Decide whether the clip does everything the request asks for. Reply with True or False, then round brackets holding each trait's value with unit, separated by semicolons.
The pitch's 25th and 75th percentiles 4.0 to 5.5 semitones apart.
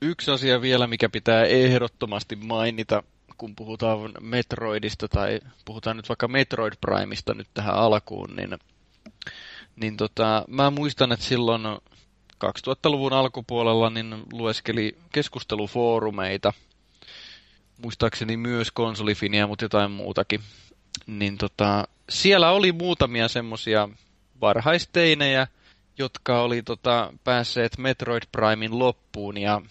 False (2.8 semitones)